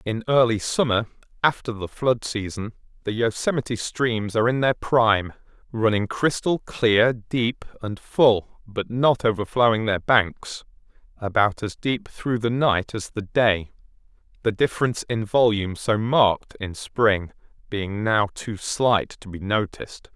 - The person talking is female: No, male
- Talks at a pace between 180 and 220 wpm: No, average, 145 wpm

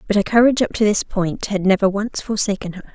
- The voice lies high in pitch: Yes, high, 205 Hz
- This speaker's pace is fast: Yes, fast, 245 wpm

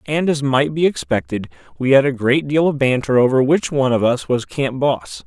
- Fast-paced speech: Yes, fast, 230 wpm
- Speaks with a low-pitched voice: Yes, low, 130 Hz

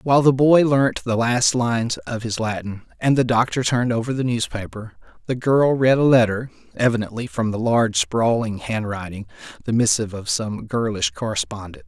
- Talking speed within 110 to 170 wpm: Yes, average, 165 wpm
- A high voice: No, low, 115 Hz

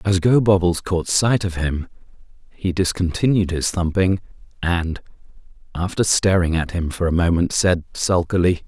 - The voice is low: Yes, very low, 90 Hz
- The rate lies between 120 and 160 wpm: Yes, average, 140 wpm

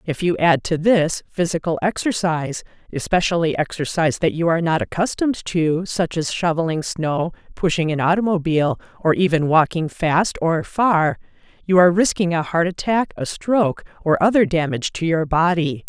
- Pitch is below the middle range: No, medium, 170 Hz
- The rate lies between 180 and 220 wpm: No, average, 150 wpm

